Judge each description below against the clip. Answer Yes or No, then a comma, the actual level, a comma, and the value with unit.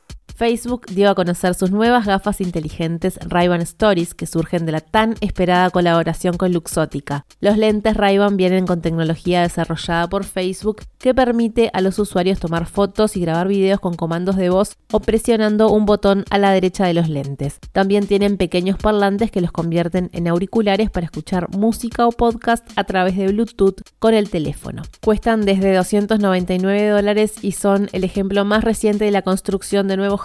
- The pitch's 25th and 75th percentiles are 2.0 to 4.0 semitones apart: Yes, average, 2.8 semitones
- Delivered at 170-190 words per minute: Yes, average, 175 wpm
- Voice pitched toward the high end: Yes, high, 195 Hz